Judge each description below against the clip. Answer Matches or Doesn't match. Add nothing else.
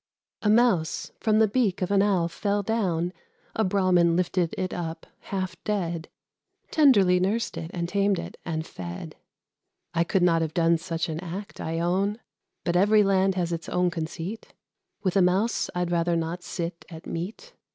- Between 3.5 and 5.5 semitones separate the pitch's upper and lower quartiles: Doesn't match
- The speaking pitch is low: Doesn't match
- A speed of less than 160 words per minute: Doesn't match